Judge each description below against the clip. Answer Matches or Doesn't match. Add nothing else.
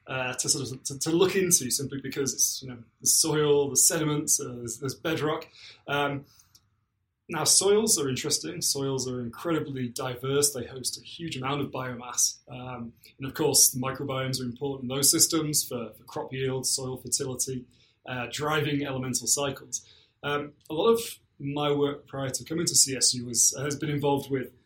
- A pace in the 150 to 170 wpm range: Doesn't match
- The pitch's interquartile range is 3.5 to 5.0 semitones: Doesn't match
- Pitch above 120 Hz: Matches